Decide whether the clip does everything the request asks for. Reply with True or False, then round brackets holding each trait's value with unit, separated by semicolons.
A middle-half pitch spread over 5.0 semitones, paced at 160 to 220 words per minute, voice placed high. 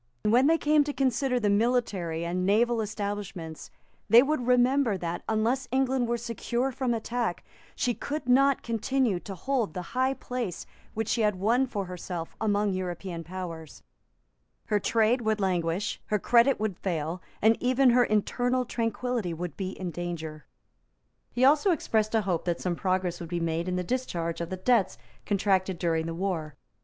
True (5.6 semitones; 170 wpm; 210 Hz)